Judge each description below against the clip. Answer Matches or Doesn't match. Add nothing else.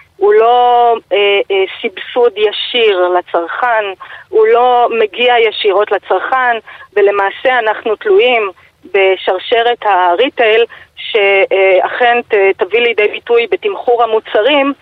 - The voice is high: Matches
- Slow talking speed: Matches